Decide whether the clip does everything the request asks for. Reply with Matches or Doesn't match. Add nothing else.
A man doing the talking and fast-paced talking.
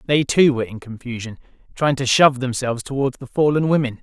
Doesn't match